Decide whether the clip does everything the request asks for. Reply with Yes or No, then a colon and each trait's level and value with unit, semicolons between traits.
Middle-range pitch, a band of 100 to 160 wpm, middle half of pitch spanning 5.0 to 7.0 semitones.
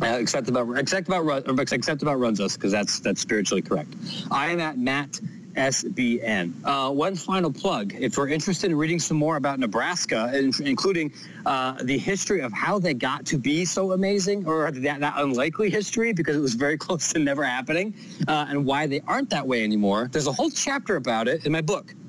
No: medium, 155 Hz; average, 200 wpm; wide, 5.5 semitones